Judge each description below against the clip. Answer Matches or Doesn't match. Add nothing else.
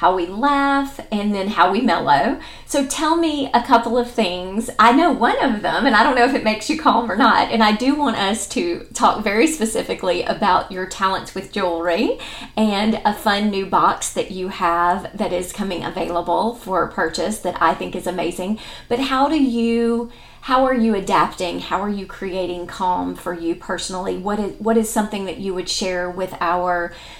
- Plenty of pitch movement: Doesn't match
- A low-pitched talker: Doesn't match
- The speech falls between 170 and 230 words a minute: Matches